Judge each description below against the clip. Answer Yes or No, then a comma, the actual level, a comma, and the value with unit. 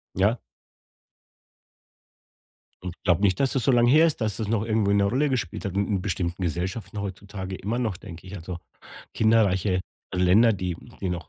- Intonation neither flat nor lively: Yes, average, 3.5 semitones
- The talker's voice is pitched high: No, low, 100 Hz